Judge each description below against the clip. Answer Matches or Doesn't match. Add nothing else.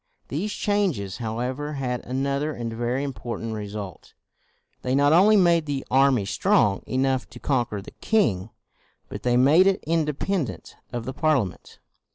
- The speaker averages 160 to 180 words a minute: Doesn't match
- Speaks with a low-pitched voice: Matches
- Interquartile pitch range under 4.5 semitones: Doesn't match